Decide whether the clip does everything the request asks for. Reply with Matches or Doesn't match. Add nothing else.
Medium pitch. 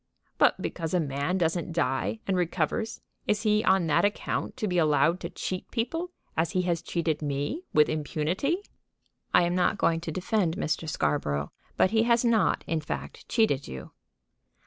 Matches